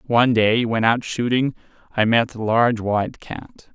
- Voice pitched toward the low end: Yes, low, 115 Hz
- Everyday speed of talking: Yes, average, 175 wpm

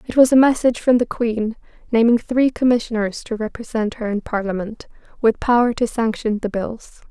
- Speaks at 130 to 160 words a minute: No, average, 175 wpm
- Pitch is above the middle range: Yes, high, 230 Hz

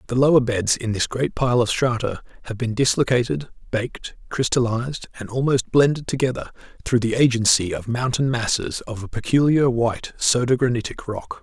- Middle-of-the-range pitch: No, low, 120 Hz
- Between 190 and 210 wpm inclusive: No, average, 165 wpm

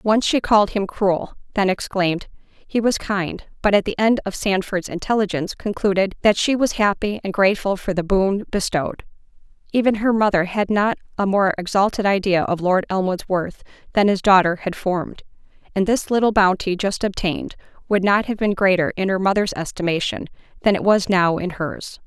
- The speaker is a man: No, female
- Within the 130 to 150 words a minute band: No, average, 180 wpm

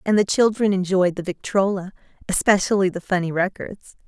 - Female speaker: Yes, female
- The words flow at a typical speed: Yes, average, 145 wpm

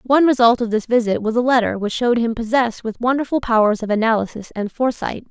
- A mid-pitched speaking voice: No, high, 230 Hz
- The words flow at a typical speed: No, fast, 215 wpm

